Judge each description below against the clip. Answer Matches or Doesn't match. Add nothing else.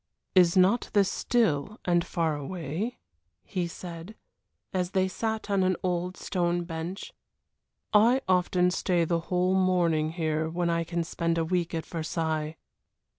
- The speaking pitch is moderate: Matches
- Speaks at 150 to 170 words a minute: Doesn't match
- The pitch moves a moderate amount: Doesn't match